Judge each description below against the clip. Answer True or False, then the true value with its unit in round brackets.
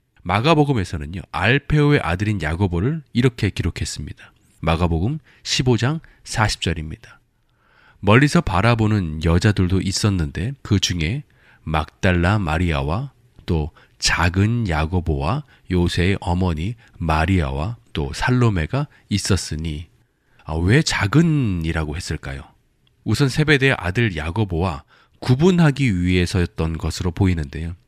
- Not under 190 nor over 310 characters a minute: True (275 characters per minute)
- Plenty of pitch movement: True (6.6 semitones)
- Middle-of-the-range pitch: False (95 Hz)